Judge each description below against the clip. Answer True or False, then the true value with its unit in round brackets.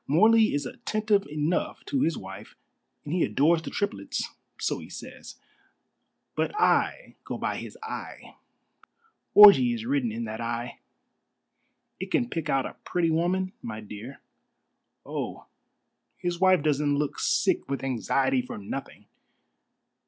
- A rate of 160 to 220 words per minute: False (135 wpm)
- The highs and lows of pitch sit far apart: True (7.2 semitones)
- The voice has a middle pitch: True (150 Hz)